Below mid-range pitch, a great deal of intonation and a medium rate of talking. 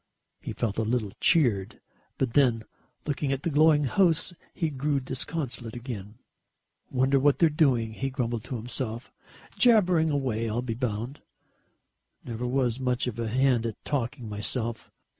No: low, 125 Hz; average, 3.7 semitones; average, 150 wpm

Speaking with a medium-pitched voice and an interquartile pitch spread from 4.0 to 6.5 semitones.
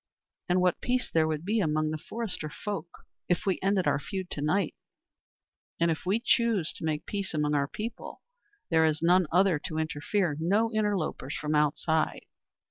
Yes: medium, 170 Hz; average, 4.4 semitones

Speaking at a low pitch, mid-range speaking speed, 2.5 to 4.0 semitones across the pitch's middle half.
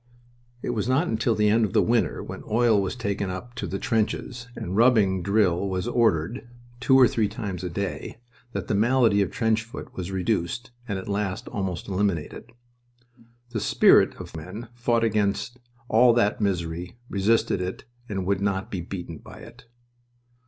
Yes: low, 105 Hz; average, 175 wpm; average, 3.6 semitones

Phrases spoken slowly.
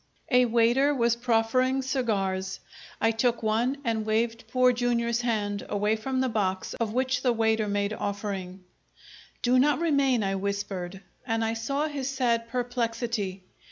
No: average, 150 wpm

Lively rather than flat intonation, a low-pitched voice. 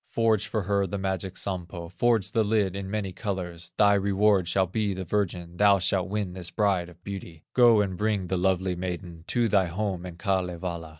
No: narrow, 2.5 semitones; very low, 95 Hz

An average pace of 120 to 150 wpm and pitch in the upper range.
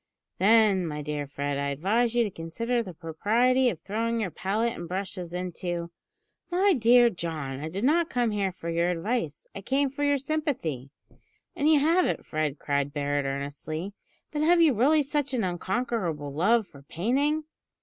No: average, 180 wpm; high, 200 Hz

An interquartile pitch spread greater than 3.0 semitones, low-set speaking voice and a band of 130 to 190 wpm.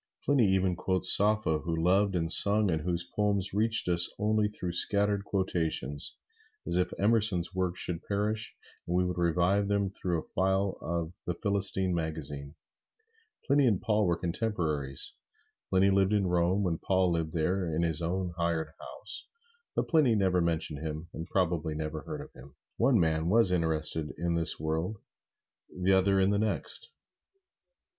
Yes: average, 3.4 semitones; very low, 90 Hz; average, 165 wpm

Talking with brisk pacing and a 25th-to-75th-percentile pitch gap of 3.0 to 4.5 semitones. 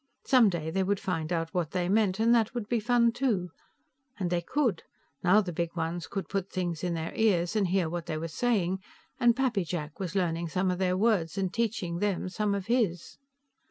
Yes: fast, 210 wpm; average, 4.0 semitones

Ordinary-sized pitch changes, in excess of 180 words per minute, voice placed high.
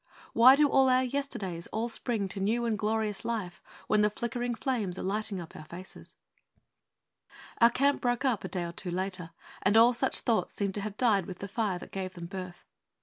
Yes: average, 4.1 semitones; fast, 205 wpm; high, 210 Hz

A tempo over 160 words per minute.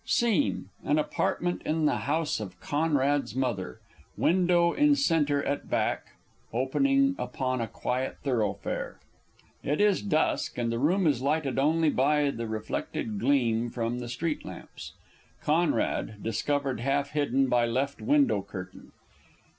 No: average, 140 wpm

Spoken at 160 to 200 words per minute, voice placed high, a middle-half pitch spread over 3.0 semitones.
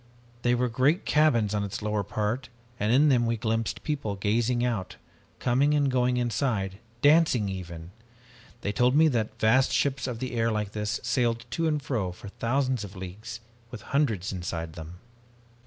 No: average, 170 wpm; low, 115 Hz; average, 4.0 semitones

